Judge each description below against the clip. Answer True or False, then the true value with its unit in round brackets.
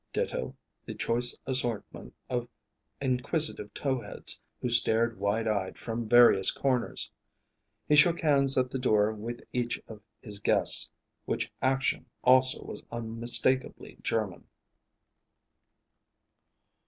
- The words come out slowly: True (115 wpm)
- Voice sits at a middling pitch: False (120 Hz)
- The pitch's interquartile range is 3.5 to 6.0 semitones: False (2.8 semitones)